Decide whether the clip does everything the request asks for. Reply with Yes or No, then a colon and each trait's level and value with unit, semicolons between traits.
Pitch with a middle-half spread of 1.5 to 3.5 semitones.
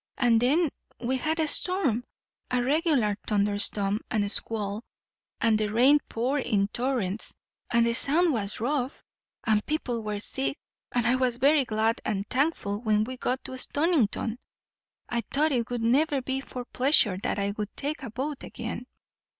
No: average, 4.2 semitones